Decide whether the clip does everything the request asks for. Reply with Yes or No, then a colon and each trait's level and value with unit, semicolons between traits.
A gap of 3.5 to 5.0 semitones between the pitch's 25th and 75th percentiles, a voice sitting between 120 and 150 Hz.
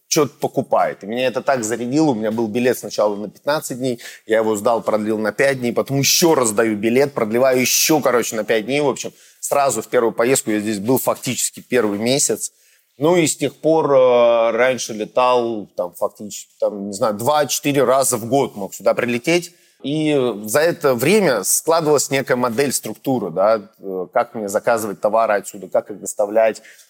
Yes: average, 4.1 semitones; low, 125 Hz